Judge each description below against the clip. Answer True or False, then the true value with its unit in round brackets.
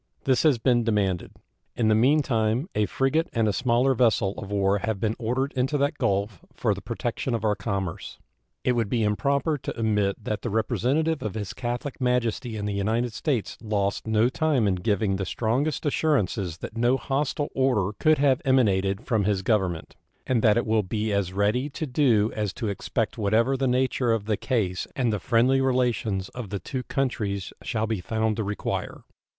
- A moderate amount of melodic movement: True (4.0 semitones)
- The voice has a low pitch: True (115 Hz)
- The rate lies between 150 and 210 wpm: True (190 wpm)